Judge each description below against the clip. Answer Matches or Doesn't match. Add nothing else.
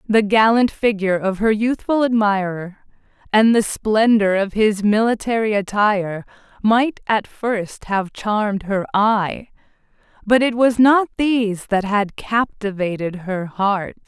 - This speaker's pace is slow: Matches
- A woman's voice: Matches